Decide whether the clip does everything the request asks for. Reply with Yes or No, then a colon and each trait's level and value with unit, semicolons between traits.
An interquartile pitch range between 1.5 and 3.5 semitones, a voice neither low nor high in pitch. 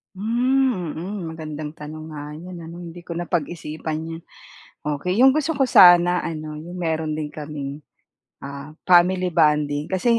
Yes: average, 3.1 semitones; medium, 165 Hz